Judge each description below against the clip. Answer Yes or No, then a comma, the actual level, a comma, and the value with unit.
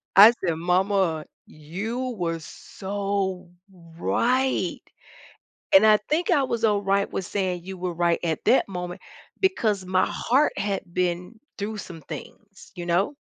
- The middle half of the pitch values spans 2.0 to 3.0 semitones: No, average, 3.4 semitones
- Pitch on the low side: No, high, 190 Hz